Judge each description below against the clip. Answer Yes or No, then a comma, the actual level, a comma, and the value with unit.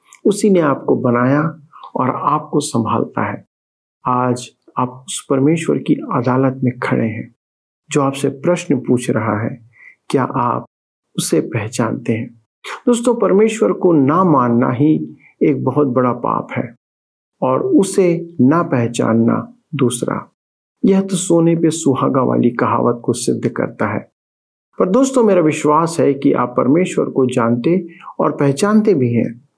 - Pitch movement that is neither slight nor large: No, wide, 6.1 semitones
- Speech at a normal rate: Yes, average, 140 wpm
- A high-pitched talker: No, low, 135 Hz